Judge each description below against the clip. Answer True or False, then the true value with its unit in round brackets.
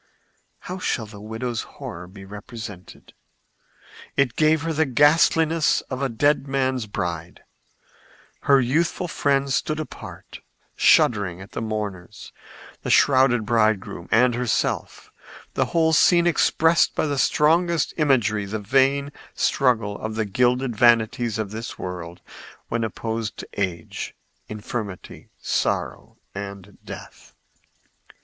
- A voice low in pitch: True (120 Hz)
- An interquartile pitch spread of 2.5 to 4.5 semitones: False (5.4 semitones)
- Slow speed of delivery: True (120 wpm)